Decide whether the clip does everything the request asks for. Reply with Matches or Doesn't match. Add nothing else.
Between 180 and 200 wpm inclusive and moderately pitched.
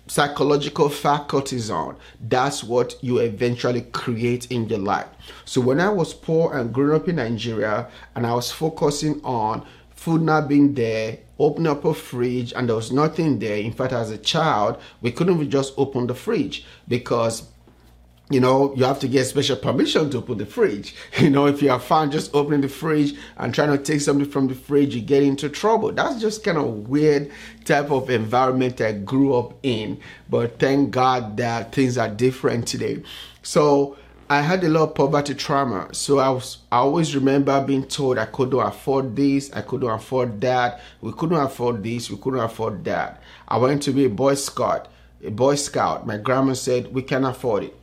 Doesn't match